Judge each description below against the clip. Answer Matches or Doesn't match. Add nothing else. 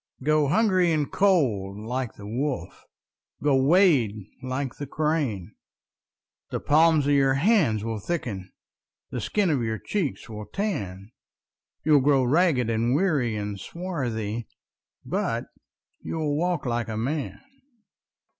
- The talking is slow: Matches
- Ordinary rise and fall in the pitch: Doesn't match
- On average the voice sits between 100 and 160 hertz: Matches